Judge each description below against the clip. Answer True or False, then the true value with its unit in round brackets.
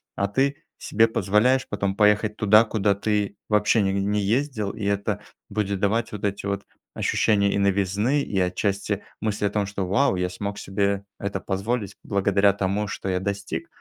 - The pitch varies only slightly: True (1.3 semitones)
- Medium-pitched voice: False (100 Hz)